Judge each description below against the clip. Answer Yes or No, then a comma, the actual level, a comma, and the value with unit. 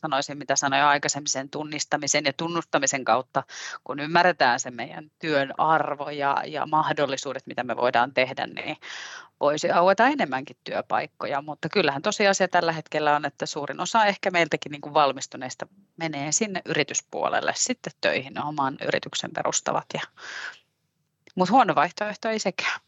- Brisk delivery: No, average, 140 wpm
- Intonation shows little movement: No, average, 3.8 semitones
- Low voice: No, medium, 155 Hz